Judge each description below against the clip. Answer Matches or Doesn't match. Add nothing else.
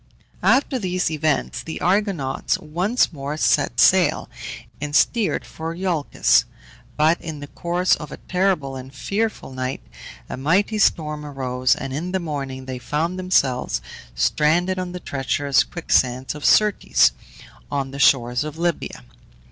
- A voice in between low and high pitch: Matches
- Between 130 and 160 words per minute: Matches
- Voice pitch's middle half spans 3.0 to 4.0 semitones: Doesn't match